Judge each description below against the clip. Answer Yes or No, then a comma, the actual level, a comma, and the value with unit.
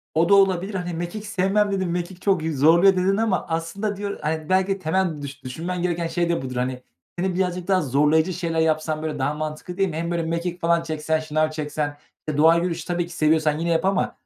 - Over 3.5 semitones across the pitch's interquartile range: No, average, 3.0 semitones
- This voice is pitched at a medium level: Yes, medium, 170 Hz